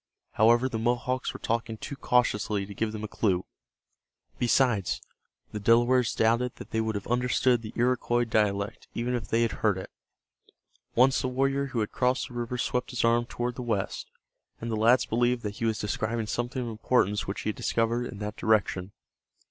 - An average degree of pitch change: No, narrow, 2.3 semitones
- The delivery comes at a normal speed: Yes, average, 190 wpm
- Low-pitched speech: Yes, low, 115 Hz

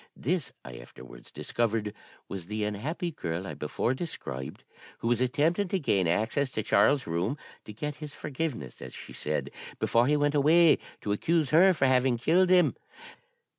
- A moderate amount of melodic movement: No, wide, 6.9 semitones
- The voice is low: Yes, low, 130 Hz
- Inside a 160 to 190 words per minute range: Yes, average, 170 wpm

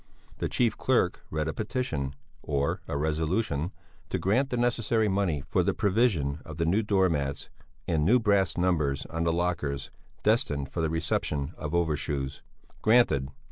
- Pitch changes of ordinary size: No, wide, 5.8 semitones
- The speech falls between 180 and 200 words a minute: No, average, 155 wpm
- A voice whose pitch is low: Yes, very low, 80 Hz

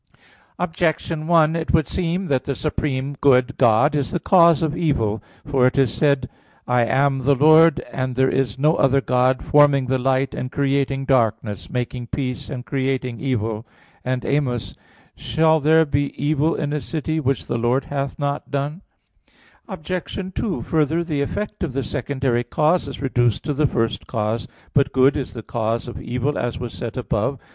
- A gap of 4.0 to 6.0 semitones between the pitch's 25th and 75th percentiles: No, average, 3.2 semitones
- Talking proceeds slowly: No, average, 185 wpm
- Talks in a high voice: No, medium, 140 Hz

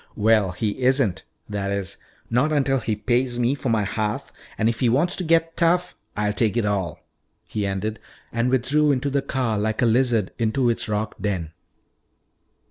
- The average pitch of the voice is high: No, low, 115 Hz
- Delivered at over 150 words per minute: Yes, average, 180 wpm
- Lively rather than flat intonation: No, average, 4.2 semitones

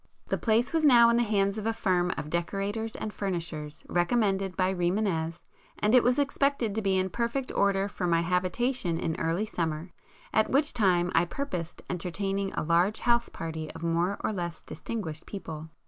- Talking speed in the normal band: Yes, average, 190 wpm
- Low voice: No, high, 195 Hz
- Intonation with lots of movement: No, average, 4.6 semitones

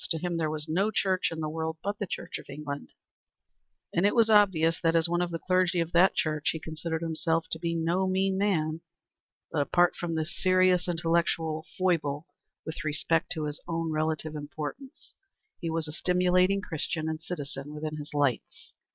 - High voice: No, medium, 165 Hz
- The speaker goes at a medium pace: Yes, average, 185 wpm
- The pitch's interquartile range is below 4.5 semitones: Yes, narrow, 2.5 semitones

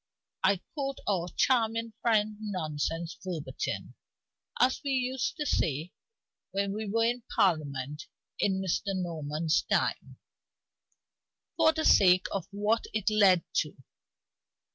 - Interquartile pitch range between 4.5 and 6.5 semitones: Yes, average, 5.2 semitones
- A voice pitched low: No, high, 200 Hz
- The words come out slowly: Yes, slow, 120 wpm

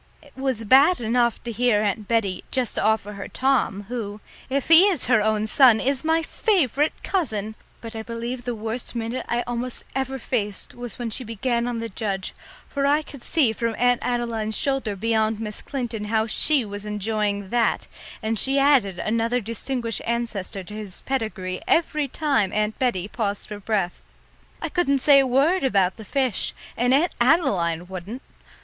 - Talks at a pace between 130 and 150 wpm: No, average, 175 wpm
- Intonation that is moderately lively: Yes, average, 3.9 semitones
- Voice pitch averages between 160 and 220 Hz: No, high, 230 Hz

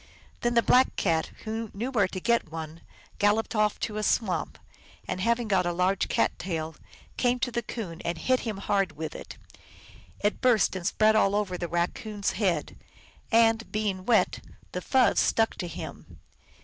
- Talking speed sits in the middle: Yes, average, 180 wpm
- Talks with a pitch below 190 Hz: No, high, 210 Hz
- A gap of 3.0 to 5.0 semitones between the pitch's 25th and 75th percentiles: Yes, average, 4.1 semitones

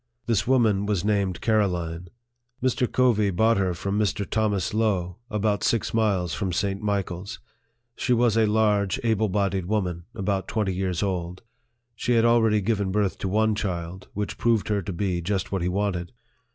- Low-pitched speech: Yes, low, 100 Hz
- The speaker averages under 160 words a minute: No, average, 170 wpm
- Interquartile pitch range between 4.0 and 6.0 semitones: No, average, 2.8 semitones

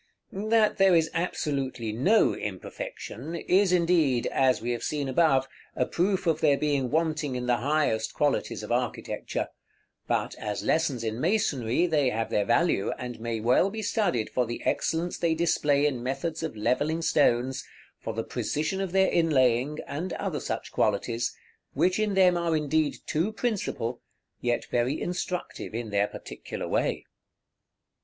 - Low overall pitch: No, medium, 150 Hz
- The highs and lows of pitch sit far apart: Yes, wide, 6.0 semitones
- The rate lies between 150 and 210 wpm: Yes, average, 155 wpm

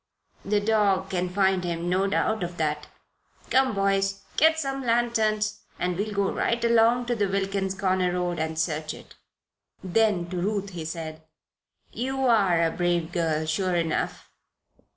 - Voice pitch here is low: No, high, 195 Hz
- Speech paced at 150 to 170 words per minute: Yes, average, 155 wpm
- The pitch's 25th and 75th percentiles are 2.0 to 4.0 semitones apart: Yes, average, 3.7 semitones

